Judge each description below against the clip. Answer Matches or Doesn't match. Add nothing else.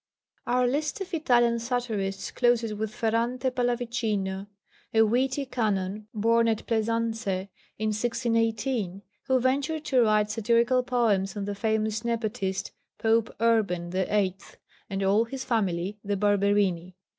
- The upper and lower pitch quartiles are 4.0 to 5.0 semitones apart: Doesn't match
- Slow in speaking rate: Matches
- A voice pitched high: Matches